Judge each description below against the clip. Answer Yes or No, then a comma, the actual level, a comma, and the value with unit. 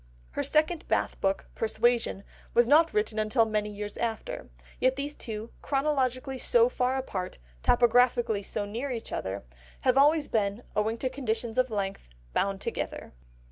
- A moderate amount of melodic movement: Yes, average, 3.9 semitones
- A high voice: Yes, high, 235 Hz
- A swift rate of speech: No, average, 150 wpm